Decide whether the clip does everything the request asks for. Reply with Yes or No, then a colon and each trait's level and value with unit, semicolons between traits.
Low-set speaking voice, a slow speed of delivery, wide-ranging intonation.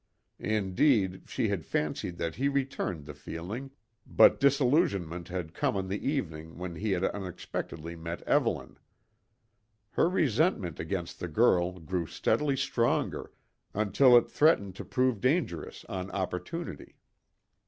Yes: very low, 95 Hz; slow, 130 wpm; wide, 7.1 semitones